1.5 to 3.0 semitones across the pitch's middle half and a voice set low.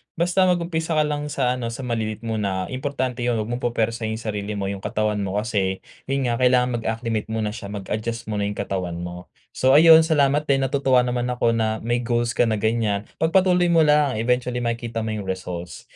No: average, 4.0 semitones; low, 115 Hz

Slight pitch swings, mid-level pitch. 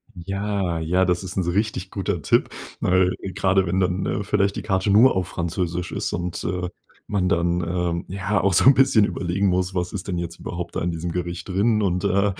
No: narrow, 2.1 semitones; very low, 90 Hz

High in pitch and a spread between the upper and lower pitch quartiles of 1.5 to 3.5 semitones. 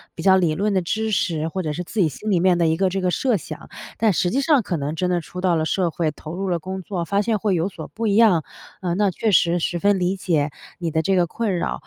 No: medium, 180 Hz; average, 3.1 semitones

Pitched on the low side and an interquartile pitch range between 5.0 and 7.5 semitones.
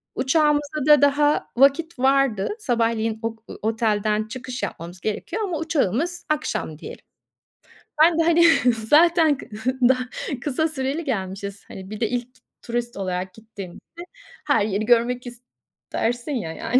No: high, 245 Hz; wide, 5.5 semitones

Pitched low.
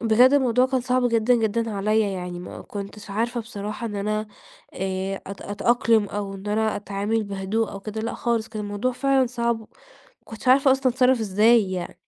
No: high, 220 Hz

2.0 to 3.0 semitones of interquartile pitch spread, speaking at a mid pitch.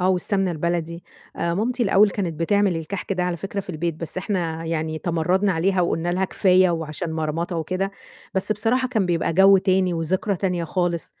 Yes: average, 2.7 semitones; medium, 180 Hz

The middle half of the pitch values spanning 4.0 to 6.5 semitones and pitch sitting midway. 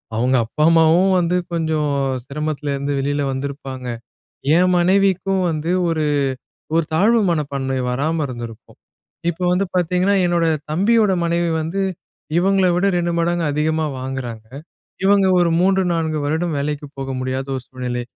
Yes: average, 4.3 semitones; medium, 160 Hz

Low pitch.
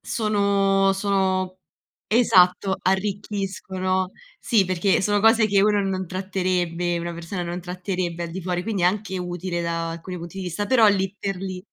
No: high, 190 Hz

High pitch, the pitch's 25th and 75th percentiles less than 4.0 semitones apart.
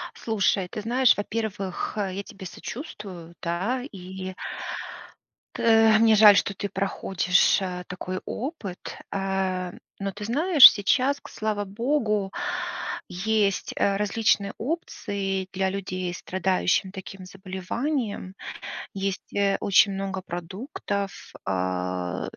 Yes: high, 195 Hz; narrow, 2.6 semitones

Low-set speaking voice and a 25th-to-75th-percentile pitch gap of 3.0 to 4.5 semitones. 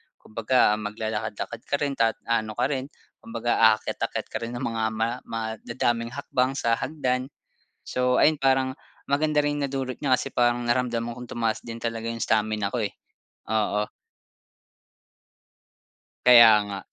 No: low, 120 Hz; narrow, 2.6 semitones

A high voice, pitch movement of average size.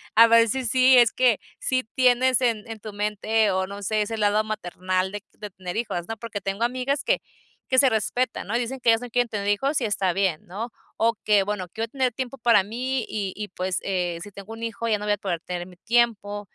Yes: high, 215 Hz; average, 3.2 semitones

